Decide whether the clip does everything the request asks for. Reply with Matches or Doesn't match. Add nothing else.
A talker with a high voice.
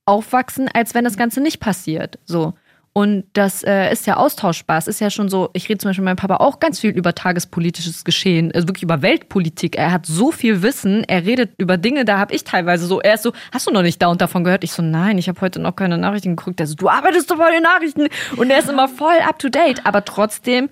Matches